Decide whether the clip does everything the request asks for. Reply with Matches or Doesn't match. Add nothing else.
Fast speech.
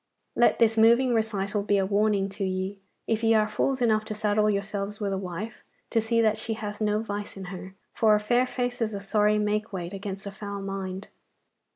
Matches